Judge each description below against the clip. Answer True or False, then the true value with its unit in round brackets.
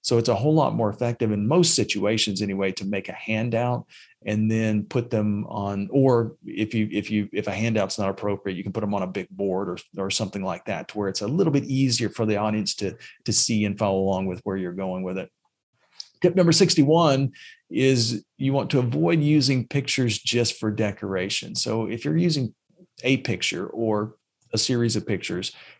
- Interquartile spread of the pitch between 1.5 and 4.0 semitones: False (4.6 semitones)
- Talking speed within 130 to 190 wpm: False (205 wpm)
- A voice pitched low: True (110 Hz)